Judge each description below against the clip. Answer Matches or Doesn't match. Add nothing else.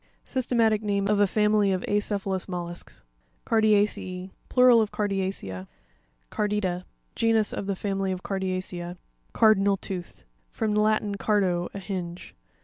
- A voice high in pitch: Matches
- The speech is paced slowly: Matches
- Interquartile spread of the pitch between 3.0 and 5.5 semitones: Doesn't match